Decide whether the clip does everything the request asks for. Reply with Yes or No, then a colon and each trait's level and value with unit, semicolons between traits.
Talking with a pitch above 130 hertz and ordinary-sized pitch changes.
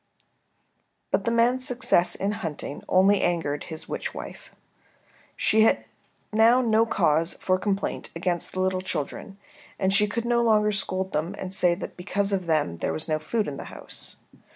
Yes: high, 190 Hz; average, 4.1 semitones